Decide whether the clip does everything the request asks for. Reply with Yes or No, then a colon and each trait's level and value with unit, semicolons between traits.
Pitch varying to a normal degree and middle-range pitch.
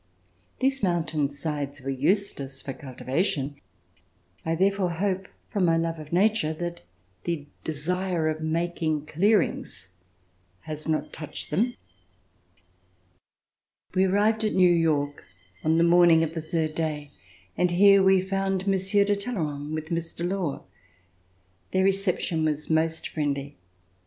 Yes: average, 3.8 semitones; medium, 165 Hz